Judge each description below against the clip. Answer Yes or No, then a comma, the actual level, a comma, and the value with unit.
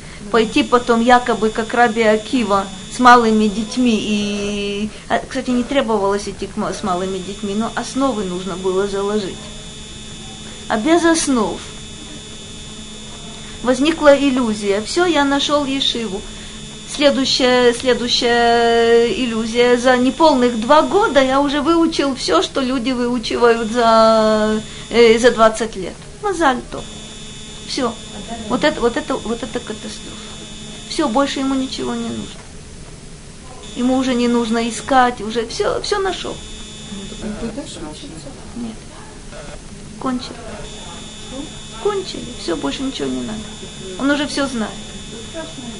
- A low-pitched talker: No, high, 235 Hz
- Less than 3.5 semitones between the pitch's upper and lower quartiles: No, average, 4.2 semitones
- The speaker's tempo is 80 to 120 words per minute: Yes, average, 115 wpm